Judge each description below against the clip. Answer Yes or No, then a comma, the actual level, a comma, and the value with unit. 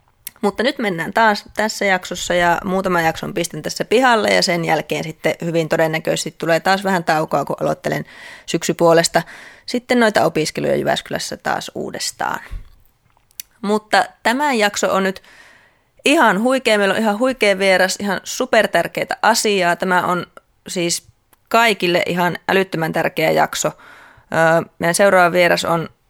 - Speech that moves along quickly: No, average, 135 wpm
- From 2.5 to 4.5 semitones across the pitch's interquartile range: Yes, average, 4.0 semitones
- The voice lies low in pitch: No, medium, 185 Hz